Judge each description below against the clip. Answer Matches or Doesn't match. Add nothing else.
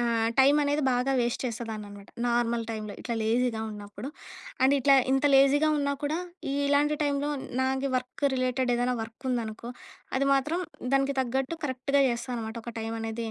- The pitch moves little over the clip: Doesn't match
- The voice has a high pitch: Matches